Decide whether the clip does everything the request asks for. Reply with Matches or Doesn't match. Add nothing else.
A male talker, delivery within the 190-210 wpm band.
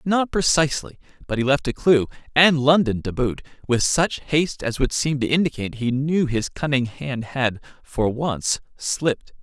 Doesn't match